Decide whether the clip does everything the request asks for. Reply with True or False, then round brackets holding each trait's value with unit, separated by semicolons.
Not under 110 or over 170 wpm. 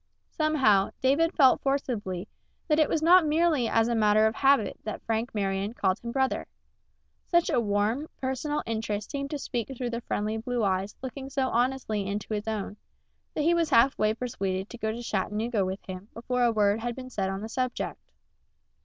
False (190 wpm)